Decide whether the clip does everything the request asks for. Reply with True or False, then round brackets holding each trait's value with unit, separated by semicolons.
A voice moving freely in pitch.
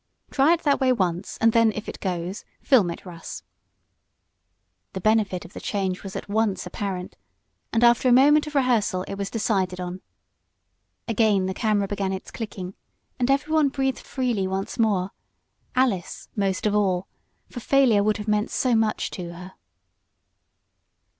False (4.2 semitones)